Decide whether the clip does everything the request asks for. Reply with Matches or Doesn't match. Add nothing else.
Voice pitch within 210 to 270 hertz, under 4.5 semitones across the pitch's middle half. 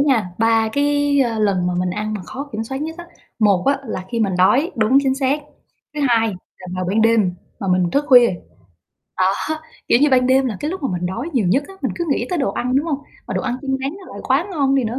Doesn't match